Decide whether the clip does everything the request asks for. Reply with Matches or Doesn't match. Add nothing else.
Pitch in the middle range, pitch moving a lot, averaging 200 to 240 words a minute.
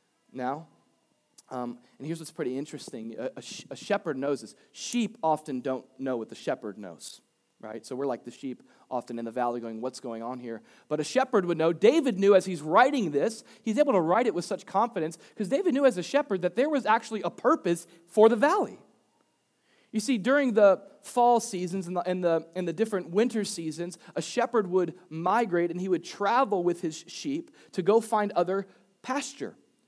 Matches